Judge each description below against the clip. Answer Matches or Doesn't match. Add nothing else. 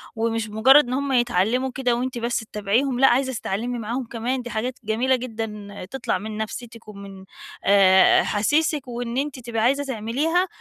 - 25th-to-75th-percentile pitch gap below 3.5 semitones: Matches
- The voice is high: Matches